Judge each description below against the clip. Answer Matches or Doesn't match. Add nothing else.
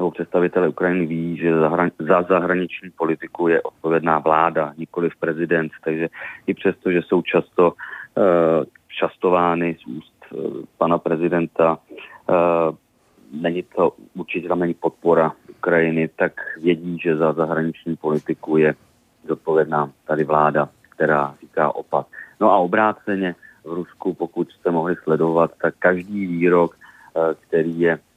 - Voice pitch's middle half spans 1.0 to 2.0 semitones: Matches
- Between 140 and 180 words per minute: Doesn't match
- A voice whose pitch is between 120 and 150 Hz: Doesn't match